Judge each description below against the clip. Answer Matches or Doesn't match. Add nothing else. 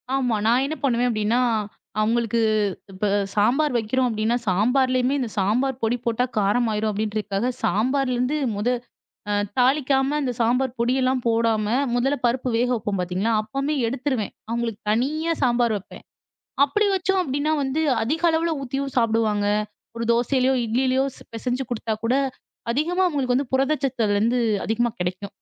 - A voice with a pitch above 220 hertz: Matches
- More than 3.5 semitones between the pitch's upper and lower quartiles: Doesn't match